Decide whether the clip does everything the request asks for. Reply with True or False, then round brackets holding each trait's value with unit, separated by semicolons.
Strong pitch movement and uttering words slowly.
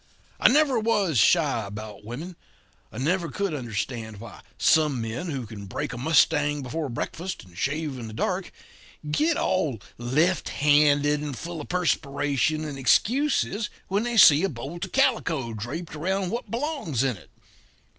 False (6.7 semitones; 160 wpm)